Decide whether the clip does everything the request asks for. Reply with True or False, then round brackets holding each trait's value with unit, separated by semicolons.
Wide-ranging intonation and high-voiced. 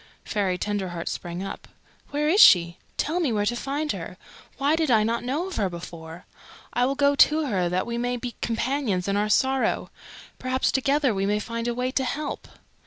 True (6.0 semitones; 240 Hz)